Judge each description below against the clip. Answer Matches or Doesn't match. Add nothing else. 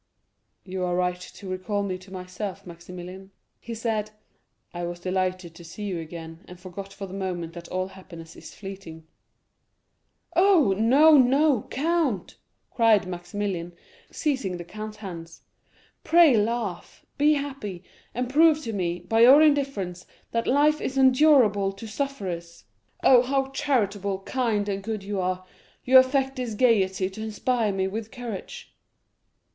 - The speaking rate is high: Doesn't match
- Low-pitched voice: Doesn't match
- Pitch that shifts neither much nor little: Doesn't match